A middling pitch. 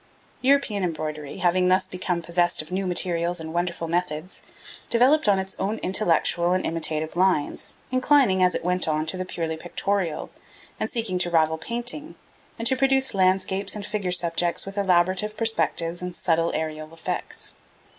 Yes: medium, 180 Hz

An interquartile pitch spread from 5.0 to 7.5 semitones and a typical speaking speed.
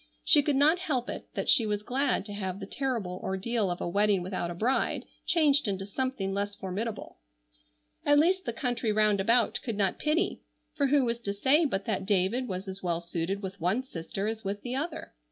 No: average, 5.3 semitones; fast, 210 wpm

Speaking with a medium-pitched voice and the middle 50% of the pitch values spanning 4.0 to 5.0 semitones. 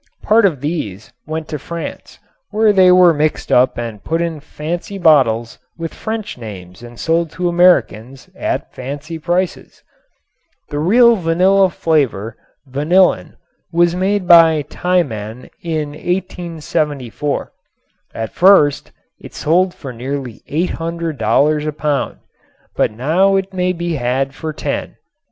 Yes: medium, 160 Hz; average, 4.7 semitones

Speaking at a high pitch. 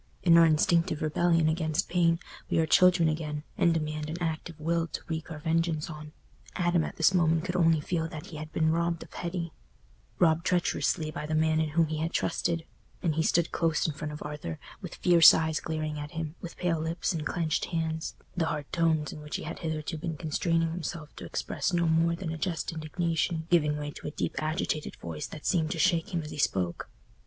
No: medium, 160 Hz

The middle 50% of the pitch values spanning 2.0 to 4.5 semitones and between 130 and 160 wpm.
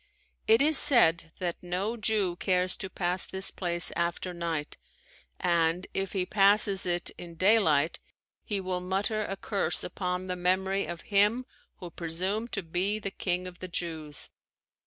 Yes: narrow, 2.4 semitones; average, 155 wpm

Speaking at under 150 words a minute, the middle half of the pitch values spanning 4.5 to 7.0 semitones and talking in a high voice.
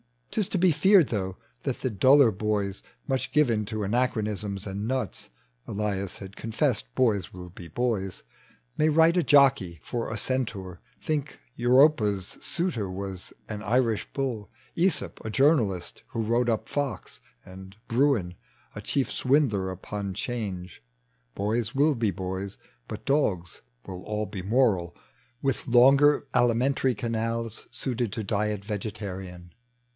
No: slow, 135 wpm; average, 5.1 semitones; low, 110 Hz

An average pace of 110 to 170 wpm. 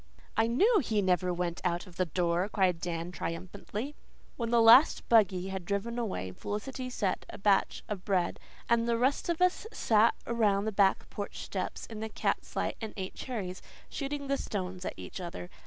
No: average, 190 wpm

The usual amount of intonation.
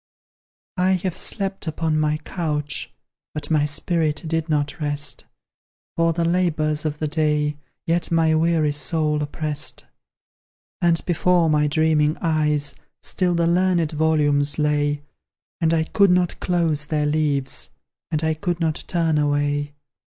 No: narrow, 2.1 semitones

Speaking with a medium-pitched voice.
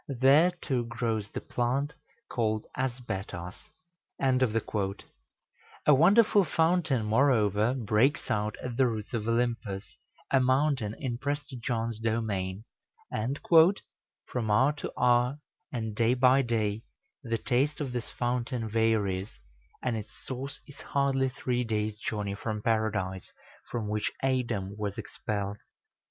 No: low, 120 Hz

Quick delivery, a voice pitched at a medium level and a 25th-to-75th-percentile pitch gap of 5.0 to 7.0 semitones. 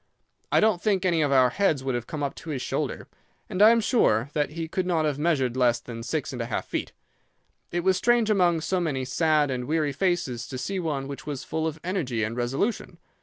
Yes: fast, 230 wpm; medium, 155 Hz; wide, 5.5 semitones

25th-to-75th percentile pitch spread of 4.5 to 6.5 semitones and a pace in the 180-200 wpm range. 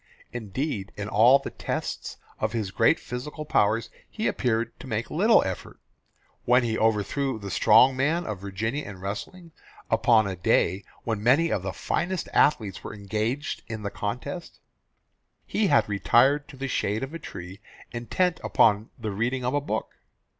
No: average, 5.1 semitones; average, 165 wpm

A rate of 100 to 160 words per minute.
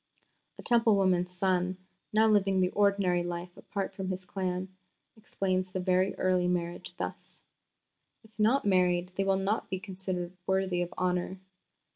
Yes: average, 150 wpm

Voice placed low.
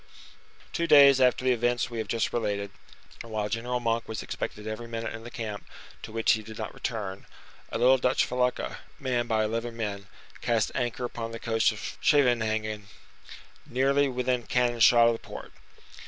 Yes: low, 115 Hz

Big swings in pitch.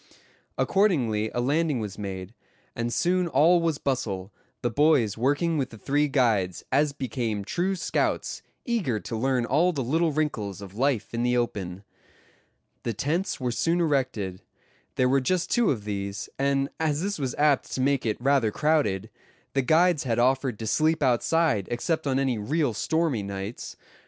Yes: wide, 5.8 semitones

